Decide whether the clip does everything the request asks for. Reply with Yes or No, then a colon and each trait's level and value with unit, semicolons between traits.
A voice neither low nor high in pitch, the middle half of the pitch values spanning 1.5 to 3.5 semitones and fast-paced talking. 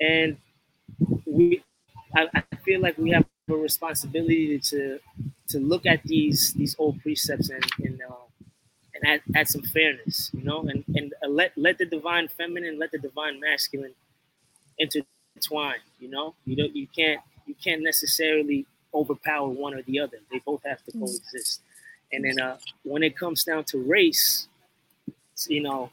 No: medium, 150 Hz; narrow, 2.5 semitones; average, 160 wpm